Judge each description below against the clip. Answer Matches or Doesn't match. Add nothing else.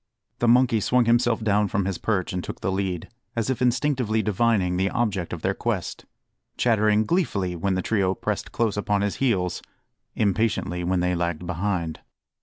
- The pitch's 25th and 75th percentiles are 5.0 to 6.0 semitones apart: Doesn't match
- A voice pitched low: Matches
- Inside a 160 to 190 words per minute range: Matches